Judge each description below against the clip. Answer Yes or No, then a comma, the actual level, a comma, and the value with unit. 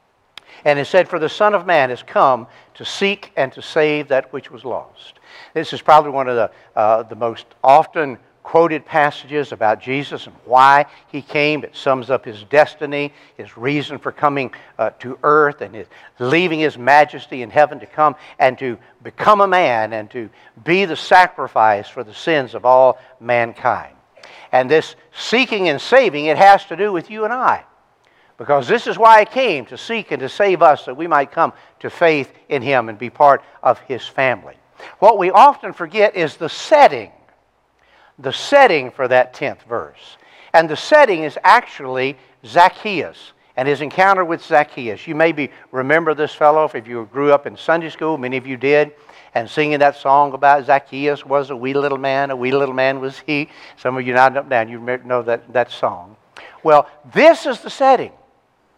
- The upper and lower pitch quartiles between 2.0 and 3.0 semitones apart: No, average, 3.8 semitones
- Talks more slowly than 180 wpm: No, average, 190 wpm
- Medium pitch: Yes, medium, 145 Hz